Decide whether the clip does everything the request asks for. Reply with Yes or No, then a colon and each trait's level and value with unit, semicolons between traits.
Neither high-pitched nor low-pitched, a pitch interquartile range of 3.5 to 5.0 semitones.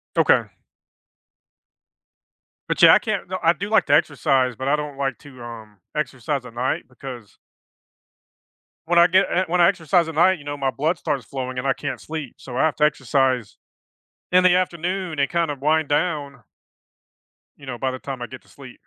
Yes: medium, 145 Hz; average, 4.4 semitones